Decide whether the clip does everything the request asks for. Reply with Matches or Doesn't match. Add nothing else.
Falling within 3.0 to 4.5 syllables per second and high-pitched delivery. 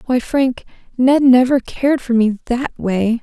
Matches